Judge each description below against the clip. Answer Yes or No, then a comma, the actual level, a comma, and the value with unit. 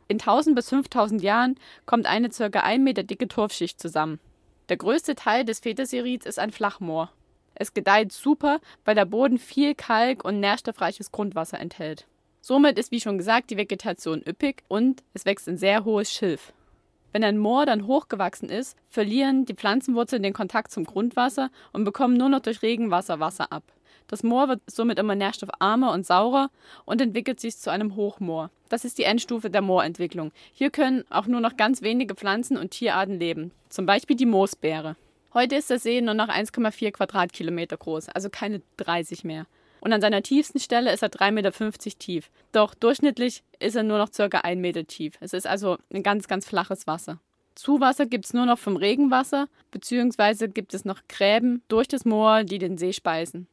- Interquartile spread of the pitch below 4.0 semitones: No, average, 4.3 semitones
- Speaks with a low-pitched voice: No, high, 215 Hz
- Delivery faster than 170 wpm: Yes, average, 185 wpm